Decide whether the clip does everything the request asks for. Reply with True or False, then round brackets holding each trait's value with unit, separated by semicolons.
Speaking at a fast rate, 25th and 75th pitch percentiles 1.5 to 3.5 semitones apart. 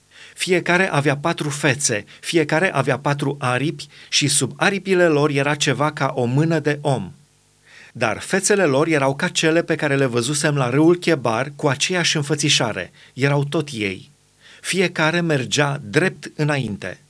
False (145 wpm; 2.8 semitones)